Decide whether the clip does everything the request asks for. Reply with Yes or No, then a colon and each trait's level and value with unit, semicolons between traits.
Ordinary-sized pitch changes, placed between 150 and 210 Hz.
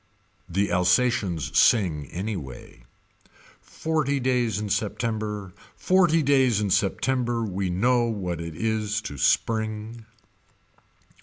No: average, 4.5 semitones; low, 110 Hz